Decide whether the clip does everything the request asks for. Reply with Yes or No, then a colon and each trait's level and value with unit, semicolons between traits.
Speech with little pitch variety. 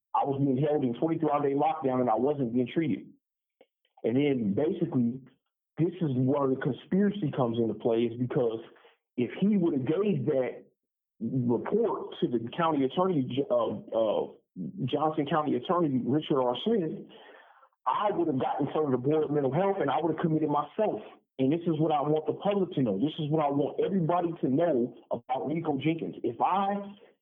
No: average, 4.4 semitones